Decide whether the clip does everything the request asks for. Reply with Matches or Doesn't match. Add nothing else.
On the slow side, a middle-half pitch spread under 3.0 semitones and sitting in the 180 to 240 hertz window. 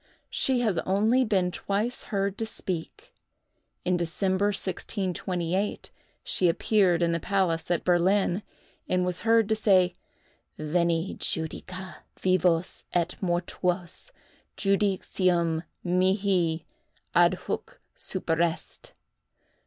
Matches